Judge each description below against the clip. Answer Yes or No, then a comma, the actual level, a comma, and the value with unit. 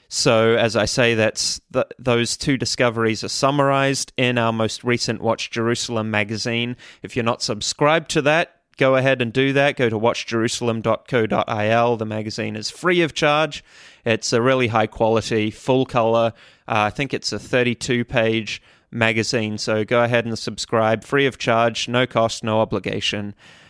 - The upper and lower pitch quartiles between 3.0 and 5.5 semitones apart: No, narrow, 2.6 semitones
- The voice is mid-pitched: No, low, 115 Hz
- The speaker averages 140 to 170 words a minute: Yes, average, 165 wpm